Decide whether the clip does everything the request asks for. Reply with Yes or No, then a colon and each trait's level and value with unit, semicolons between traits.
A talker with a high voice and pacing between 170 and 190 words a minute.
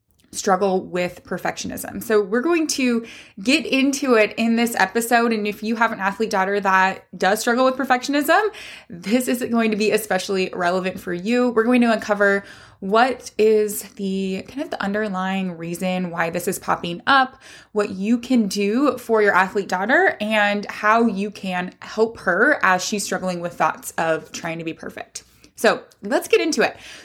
Yes: high, 210 Hz; average, 175 wpm